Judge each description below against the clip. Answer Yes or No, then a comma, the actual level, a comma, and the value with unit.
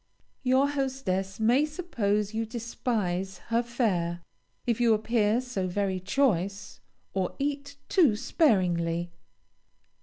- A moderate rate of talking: No, slow, 110 wpm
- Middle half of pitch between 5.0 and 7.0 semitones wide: Yes, average, 5.3 semitones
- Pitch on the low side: No, high, 220 Hz